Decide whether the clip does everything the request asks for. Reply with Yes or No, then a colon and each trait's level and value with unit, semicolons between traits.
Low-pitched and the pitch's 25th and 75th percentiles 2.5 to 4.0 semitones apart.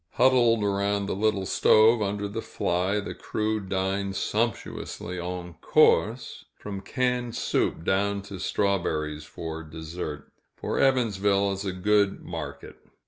Yes: low, 100 Hz; average, 2.8 semitones